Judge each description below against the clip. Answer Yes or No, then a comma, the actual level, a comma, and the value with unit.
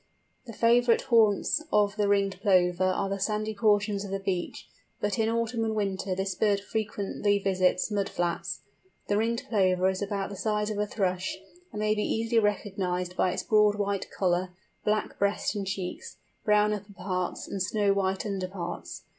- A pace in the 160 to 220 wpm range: Yes, average, 180 wpm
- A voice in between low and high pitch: No, high, 200 Hz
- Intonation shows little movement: Yes, narrow, 1.9 semitones